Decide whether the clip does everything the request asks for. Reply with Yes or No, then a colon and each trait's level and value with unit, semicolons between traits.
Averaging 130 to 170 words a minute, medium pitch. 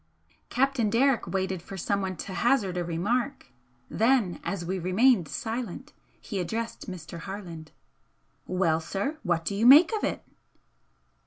No: average, 140 wpm; high, 200 Hz